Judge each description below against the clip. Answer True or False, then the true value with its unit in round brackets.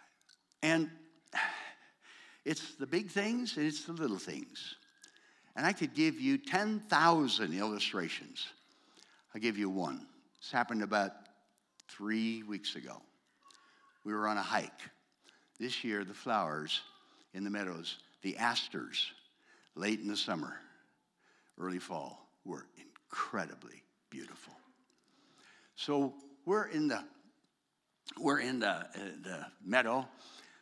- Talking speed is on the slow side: True (120 wpm)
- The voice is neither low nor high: True (150 Hz)